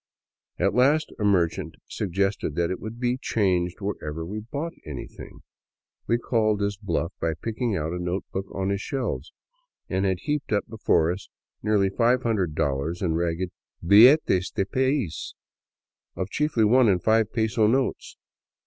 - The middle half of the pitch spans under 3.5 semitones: No, average, 4.7 semitones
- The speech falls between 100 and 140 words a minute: No, average, 155 wpm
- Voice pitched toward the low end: Yes, low, 100 Hz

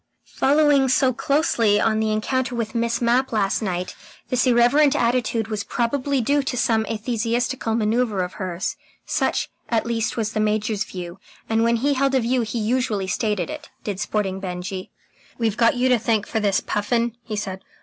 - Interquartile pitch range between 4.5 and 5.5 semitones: No, average, 2.9 semitones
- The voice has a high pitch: Yes, high, 230 Hz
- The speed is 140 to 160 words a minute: No, average, 180 wpm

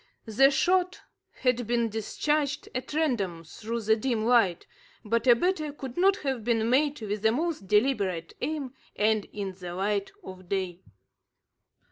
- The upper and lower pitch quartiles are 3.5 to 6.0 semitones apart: Yes, average, 5.1 semitones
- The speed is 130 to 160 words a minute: Yes, average, 150 wpm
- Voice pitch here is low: No, high, 230 Hz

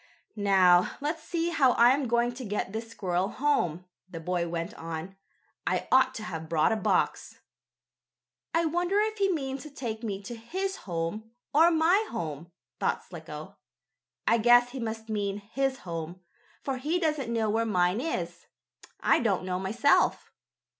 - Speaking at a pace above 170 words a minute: No, average, 165 wpm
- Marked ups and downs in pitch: Yes, wide, 7.1 semitones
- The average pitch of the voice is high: Yes, high, 225 Hz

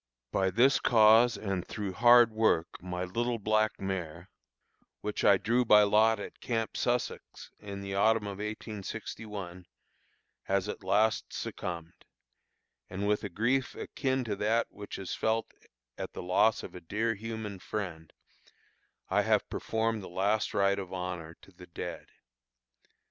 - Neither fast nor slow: Yes, average, 150 wpm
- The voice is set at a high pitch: No, low, 105 Hz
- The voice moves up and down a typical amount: Yes, average, 3.0 semitones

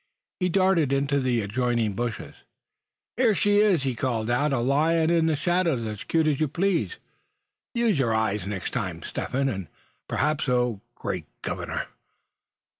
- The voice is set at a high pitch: No, low, 135 Hz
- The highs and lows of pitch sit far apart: Yes, wide, 6.1 semitones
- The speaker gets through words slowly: No, average, 160 wpm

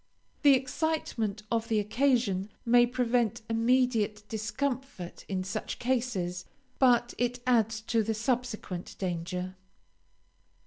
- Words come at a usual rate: No, slow, 105 wpm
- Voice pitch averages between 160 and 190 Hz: No, high, 230 Hz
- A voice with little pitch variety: No, average, 3.2 semitones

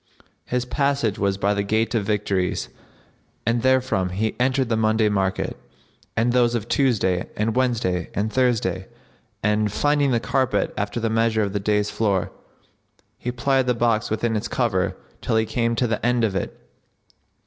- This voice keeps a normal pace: Yes, average, 170 wpm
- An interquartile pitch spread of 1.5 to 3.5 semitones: Yes, average, 3.2 semitones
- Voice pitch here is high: No, low, 110 Hz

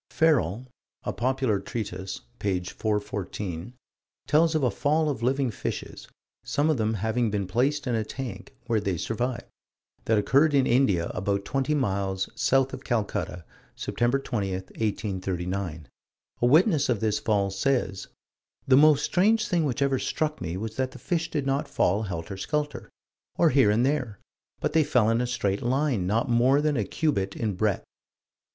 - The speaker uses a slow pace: No, average, 165 wpm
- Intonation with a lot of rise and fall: Yes, wide, 5.7 semitones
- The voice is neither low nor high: No, low, 120 Hz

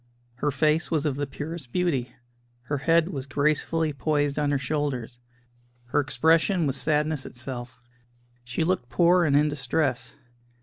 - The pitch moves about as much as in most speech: Yes, average, 3.1 semitones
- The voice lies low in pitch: No, medium, 145 Hz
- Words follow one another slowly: No, average, 145 wpm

